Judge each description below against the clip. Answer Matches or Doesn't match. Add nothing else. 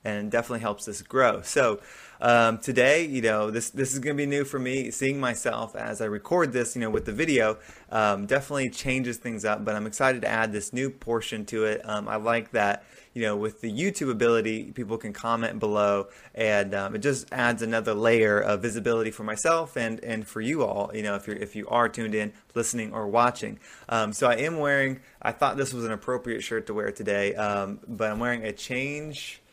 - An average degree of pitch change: Matches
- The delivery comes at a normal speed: Doesn't match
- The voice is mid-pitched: Doesn't match